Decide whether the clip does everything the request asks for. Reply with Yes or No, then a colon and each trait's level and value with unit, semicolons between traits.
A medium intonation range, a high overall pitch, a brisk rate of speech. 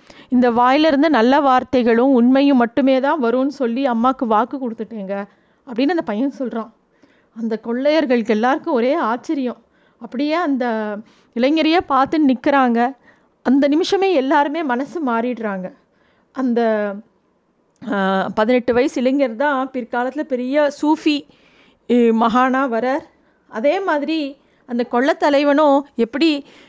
No: average, 3.5 semitones; very high, 260 Hz; average, 105 wpm